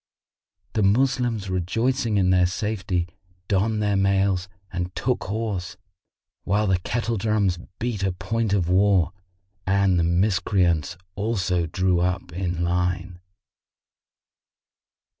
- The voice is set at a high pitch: No, very low, 95 Hz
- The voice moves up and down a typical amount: Yes, average, 3.0 semitones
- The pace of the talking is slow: Yes, slow, 115 wpm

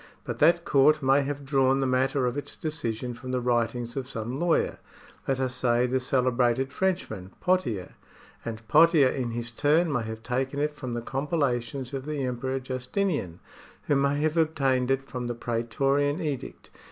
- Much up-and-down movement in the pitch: No, average, 3.0 semitones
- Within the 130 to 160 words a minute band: No, average, 175 wpm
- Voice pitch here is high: No, low, 130 Hz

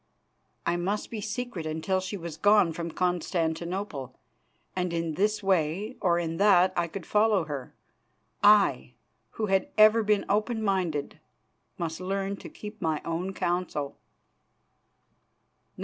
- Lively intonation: No, average, 3.8 semitones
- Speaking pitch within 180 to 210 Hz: Yes, medium, 185 Hz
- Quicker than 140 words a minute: No, slow, 135 wpm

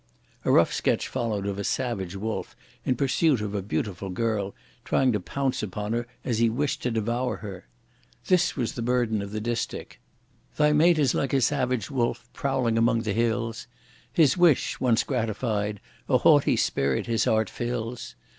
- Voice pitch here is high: No, low, 115 Hz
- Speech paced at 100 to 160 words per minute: No, average, 175 wpm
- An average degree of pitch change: Yes, average, 3.4 semitones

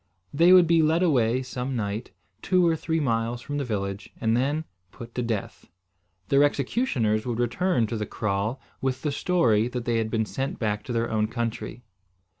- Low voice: Yes, low, 120 Hz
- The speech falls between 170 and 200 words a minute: Yes, average, 190 wpm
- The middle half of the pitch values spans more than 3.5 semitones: Yes, average, 4.5 semitones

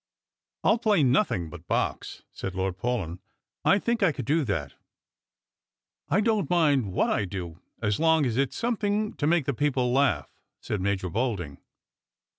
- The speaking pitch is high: No, low, 130 Hz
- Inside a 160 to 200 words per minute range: Yes, average, 175 wpm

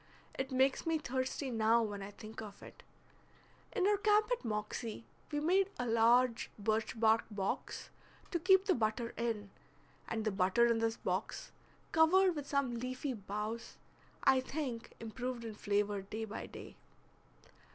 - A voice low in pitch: No, high, 235 Hz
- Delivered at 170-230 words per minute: No, average, 155 wpm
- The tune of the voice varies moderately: Yes, average, 4.3 semitones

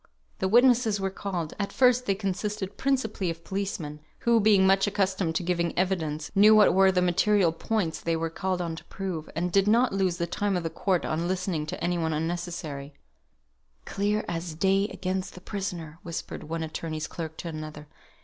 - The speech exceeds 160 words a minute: Yes, average, 190 wpm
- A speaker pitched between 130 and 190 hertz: Yes, medium, 185 Hz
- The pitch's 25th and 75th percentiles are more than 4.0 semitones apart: No, average, 3.3 semitones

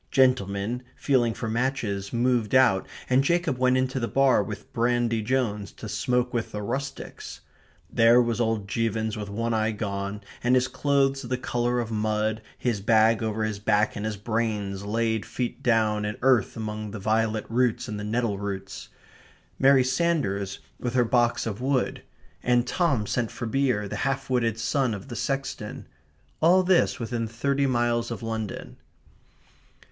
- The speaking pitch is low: Yes, low, 115 Hz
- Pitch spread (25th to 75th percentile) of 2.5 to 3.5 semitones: Yes, average, 3.0 semitones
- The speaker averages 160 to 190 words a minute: Yes, average, 165 wpm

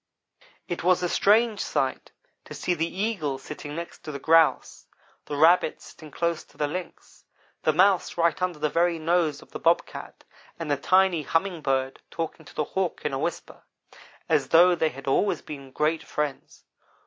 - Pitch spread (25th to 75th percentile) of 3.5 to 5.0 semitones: No, average, 3.1 semitones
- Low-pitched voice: No, medium, 165 Hz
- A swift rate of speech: No, average, 180 wpm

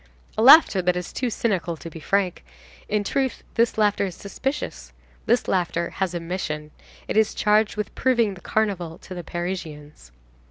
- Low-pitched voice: No, high, 190 Hz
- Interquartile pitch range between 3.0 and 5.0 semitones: Yes, average, 4.1 semitones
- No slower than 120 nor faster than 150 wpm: No, average, 170 wpm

